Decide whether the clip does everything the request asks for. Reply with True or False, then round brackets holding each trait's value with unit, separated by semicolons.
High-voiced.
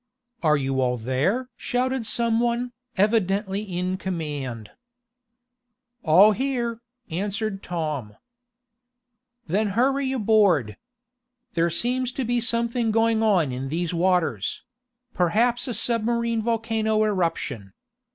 True (210 Hz)